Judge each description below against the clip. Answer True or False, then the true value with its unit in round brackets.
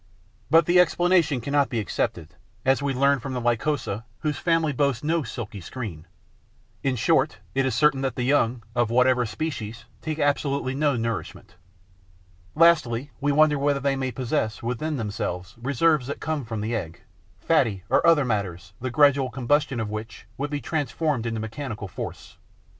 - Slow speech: False (165 wpm)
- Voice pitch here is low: True (130 Hz)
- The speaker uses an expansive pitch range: False (4.2 semitones)